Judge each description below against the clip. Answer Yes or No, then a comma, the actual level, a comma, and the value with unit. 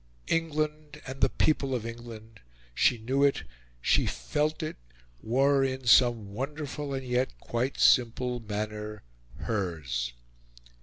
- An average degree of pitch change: Yes, average, 4.2 semitones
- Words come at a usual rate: No, slow, 120 wpm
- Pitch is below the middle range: Yes, low, 125 Hz